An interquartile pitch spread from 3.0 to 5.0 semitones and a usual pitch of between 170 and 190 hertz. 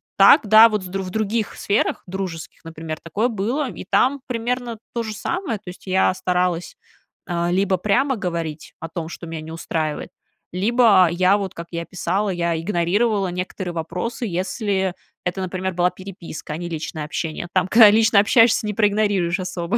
Yes: average, 3.7 semitones; medium, 185 Hz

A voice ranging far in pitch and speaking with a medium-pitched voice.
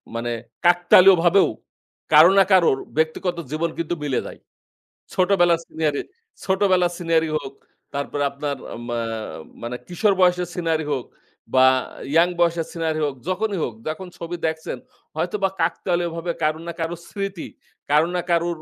No: narrow, 2.4 semitones; medium, 170 Hz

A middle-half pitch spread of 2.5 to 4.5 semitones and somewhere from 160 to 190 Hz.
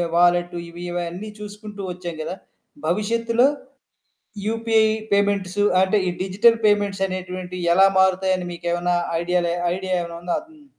Yes: average, 2.9 semitones; medium, 185 Hz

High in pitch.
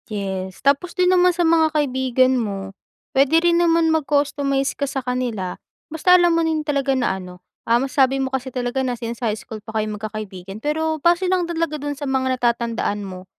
Yes: very high, 265 Hz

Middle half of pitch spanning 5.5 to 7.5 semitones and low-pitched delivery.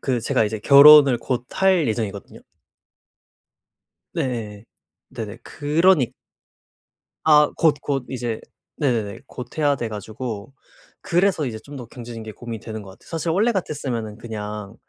No: average, 5.1 semitones; low, 120 Hz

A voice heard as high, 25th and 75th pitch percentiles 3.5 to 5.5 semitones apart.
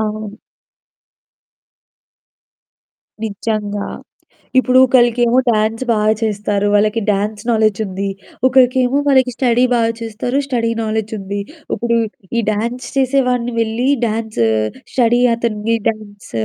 No: high, 225 Hz; narrow, 2.5 semitones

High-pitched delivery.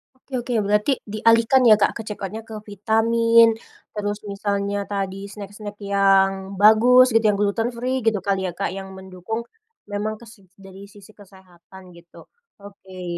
Yes: high, 205 Hz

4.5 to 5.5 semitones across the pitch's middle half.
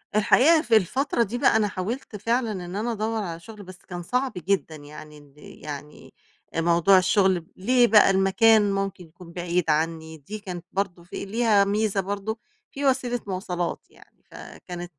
No: average, 4.1 semitones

